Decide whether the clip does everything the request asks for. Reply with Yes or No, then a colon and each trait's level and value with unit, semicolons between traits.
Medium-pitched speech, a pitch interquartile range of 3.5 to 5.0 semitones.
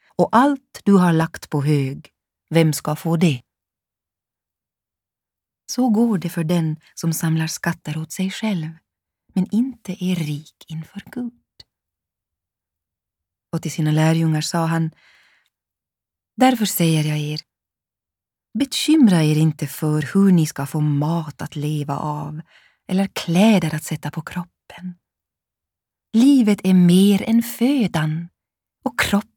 Yes: medium, 160 Hz; average, 4.4 semitones